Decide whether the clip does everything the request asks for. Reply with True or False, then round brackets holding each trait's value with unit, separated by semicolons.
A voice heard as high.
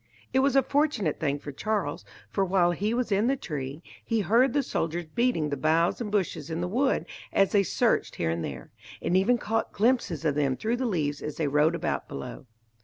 False (180 Hz)